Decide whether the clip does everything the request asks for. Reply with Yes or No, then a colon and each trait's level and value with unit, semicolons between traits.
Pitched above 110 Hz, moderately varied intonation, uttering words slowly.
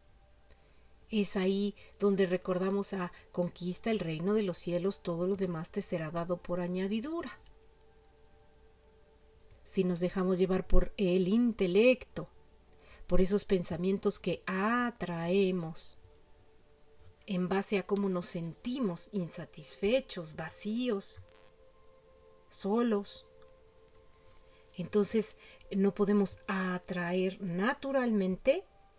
Yes: medium, 185 Hz; average, 3.1 semitones; slow, 95 wpm